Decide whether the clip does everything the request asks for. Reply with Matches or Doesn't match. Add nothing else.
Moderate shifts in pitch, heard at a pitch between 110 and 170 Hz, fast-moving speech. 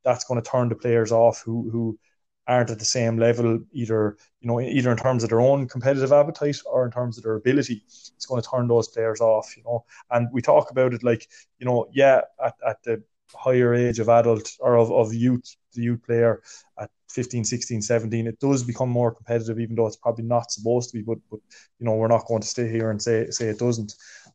Doesn't match